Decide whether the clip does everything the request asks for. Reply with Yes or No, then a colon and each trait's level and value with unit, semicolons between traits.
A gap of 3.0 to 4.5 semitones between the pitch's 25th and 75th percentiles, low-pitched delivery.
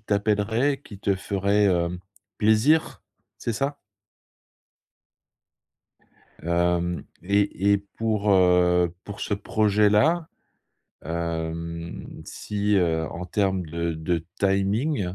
Yes: average, 3.4 semitones; low, 100 Hz